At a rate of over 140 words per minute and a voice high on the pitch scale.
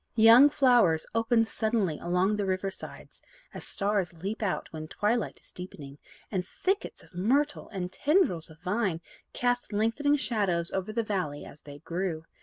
Yes: average, 160 wpm; high, 200 Hz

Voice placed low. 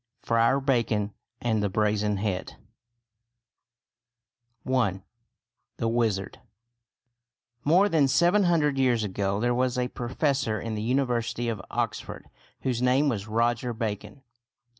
Yes: low, 120 Hz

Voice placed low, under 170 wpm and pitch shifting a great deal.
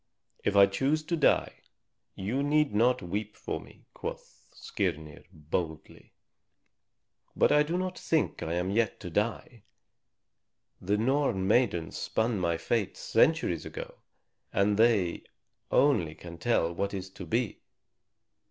Yes: low, 105 Hz; slow, 135 wpm; wide, 6.1 semitones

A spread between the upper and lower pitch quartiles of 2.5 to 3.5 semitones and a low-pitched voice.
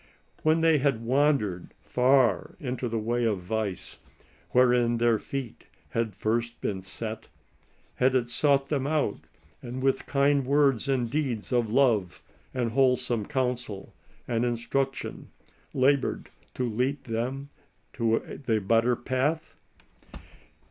Yes: average, 3.1 semitones; low, 125 Hz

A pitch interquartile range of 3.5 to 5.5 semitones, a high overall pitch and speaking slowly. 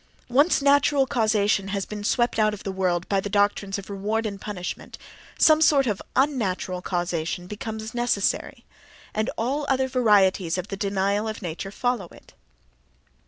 No: average, 3.9 semitones; high, 210 Hz; average, 160 wpm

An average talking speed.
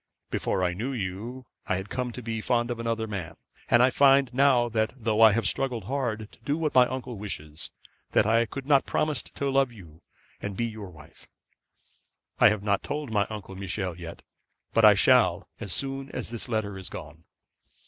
Yes: average, 190 wpm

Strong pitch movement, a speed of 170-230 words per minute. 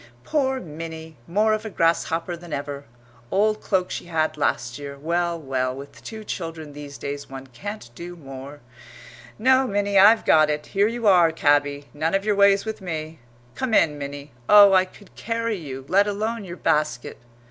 Yes: wide, 5.8 semitones; average, 180 wpm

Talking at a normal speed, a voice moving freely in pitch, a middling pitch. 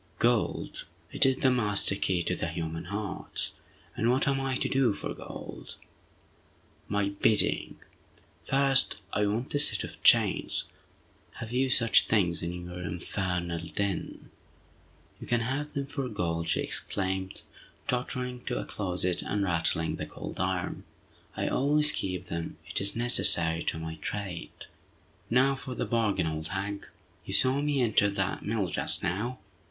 No: average, 150 wpm; wide, 6.0 semitones; low, 100 Hz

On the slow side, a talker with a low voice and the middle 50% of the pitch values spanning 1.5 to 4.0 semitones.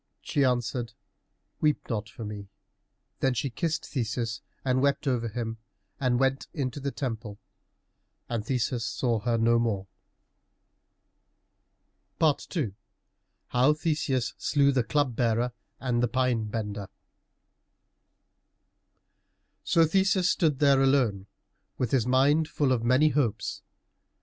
Yes: slow, 120 wpm; low, 125 Hz; average, 3.5 semitones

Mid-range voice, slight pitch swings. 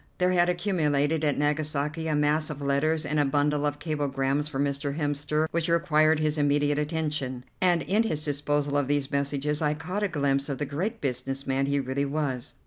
Yes: medium, 145 Hz; narrow, 1.8 semitones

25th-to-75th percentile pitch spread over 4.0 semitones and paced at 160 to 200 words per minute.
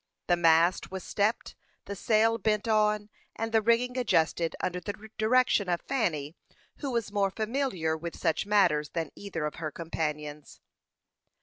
No: average, 5.0 semitones; average, 150 wpm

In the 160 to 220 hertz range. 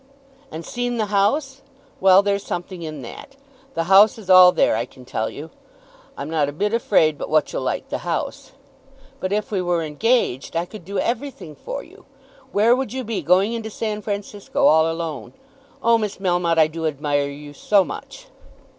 Yes: high, 190 Hz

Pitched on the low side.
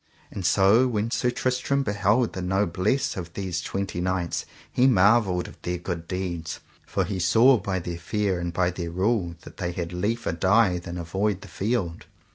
Yes: very low, 95 Hz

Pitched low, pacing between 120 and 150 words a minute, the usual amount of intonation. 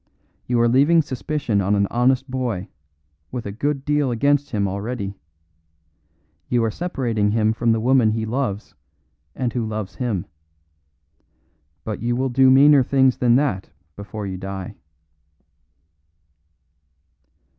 Yes: low, 120 Hz; slow, 135 wpm; average, 3.9 semitones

